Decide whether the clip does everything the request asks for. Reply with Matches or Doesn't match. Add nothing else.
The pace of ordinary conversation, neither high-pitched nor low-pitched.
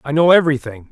Matches